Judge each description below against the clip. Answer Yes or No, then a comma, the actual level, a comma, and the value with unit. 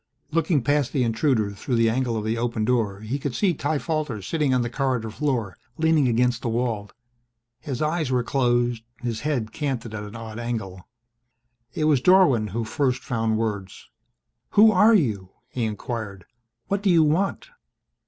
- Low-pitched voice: Yes, low, 120 Hz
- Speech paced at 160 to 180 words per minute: Yes, average, 175 wpm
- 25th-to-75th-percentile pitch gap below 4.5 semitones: No, average, 5.0 semitones